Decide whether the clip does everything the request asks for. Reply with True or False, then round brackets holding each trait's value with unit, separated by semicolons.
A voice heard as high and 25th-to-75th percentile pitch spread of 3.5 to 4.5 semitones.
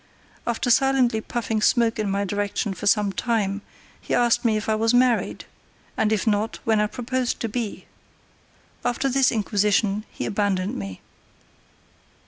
False (220 Hz; 2.7 semitones)